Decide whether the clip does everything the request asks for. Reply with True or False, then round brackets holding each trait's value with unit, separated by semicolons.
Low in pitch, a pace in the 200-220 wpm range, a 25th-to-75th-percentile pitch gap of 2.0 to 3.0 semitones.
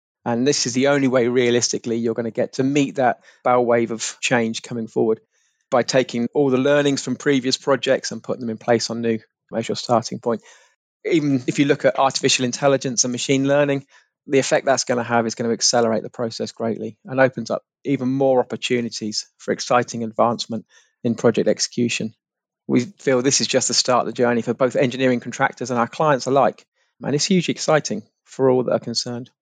True (125 Hz; 205 wpm; 2.5 semitones)